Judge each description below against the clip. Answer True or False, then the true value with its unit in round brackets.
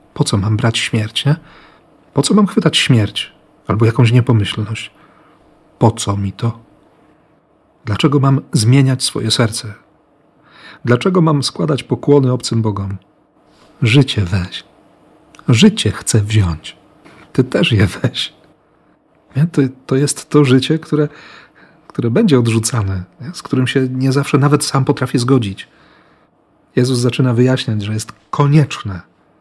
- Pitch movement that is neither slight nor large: True (4.7 semitones)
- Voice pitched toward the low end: True (130 Hz)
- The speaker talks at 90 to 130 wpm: True (125 wpm)